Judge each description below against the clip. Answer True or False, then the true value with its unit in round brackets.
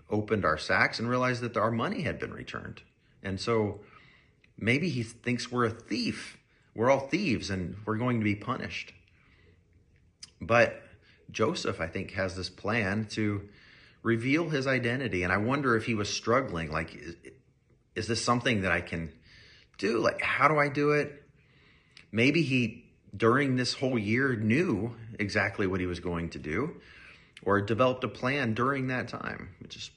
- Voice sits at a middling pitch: False (115 Hz)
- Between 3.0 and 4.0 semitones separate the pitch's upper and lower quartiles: False (4.4 semitones)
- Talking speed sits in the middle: True (170 wpm)